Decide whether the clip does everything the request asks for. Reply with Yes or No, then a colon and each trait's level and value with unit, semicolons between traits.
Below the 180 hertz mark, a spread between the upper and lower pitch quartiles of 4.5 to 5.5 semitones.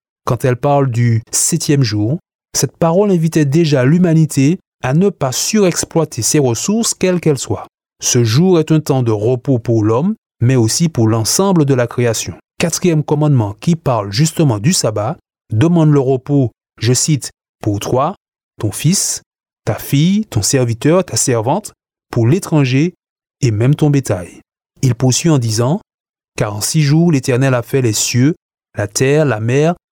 Yes: medium, 140 Hz; average, 5.1 semitones